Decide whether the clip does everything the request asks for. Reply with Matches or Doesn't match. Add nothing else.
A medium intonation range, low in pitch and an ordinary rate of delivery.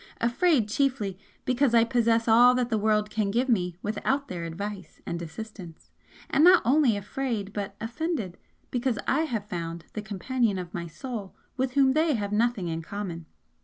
Doesn't match